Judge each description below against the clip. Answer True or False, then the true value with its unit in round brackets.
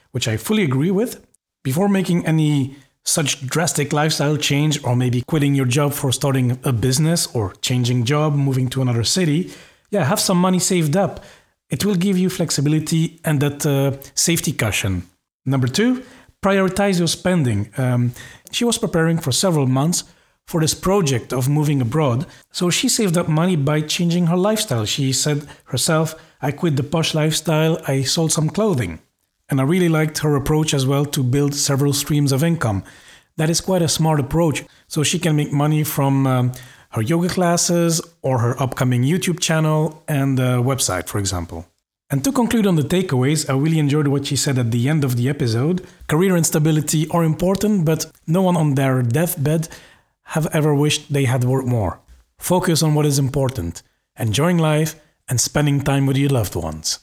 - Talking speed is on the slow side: False (180 wpm)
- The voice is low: False (150 Hz)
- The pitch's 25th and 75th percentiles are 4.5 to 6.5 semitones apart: False (4.0 semitones)